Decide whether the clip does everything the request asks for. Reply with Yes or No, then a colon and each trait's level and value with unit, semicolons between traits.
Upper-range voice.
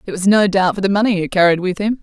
Yes: high, 195 Hz